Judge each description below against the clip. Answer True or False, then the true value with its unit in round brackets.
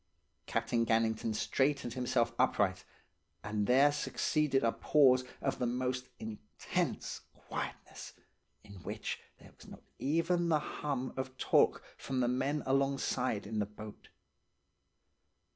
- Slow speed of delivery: True (125 wpm)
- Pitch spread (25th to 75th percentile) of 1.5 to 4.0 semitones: True (3.6 semitones)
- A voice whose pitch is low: True (125 Hz)